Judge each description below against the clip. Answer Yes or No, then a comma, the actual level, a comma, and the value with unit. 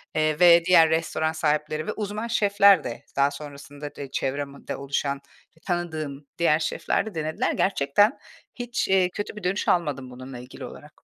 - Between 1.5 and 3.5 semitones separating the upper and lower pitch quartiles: No, average, 4.4 semitones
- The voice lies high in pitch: No, medium, 155 Hz